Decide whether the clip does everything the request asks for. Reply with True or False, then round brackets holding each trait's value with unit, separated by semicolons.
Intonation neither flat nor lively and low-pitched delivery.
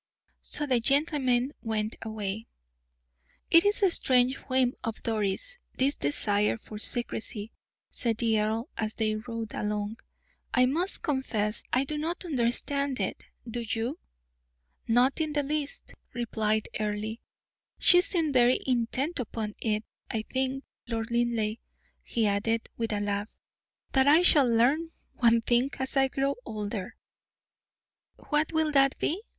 False (4.1 semitones; 240 Hz)